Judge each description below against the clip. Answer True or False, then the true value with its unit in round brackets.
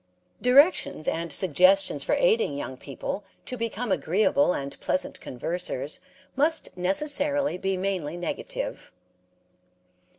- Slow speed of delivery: True (105 wpm)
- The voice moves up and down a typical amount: False (8.3 semitones)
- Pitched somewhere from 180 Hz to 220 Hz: True (190 Hz)